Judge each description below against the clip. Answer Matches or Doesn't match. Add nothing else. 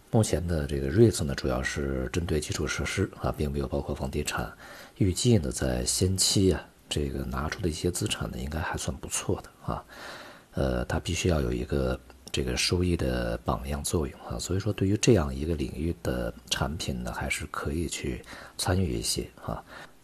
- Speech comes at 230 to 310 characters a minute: Matches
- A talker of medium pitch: Doesn't match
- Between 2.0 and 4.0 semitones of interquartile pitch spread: Doesn't match